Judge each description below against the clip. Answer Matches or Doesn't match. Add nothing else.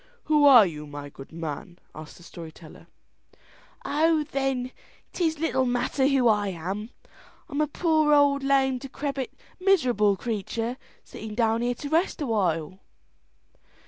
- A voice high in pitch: Matches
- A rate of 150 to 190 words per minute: Doesn't match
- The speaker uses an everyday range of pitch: Doesn't match